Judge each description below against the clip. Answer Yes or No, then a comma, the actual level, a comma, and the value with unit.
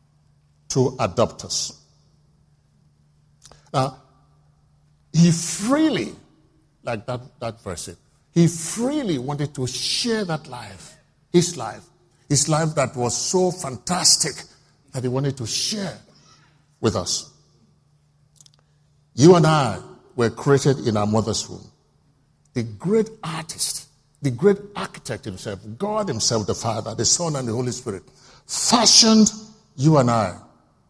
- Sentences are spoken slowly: Yes, slow, 120 wpm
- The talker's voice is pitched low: No, medium, 145 Hz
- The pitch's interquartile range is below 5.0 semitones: Yes, average, 4.4 semitones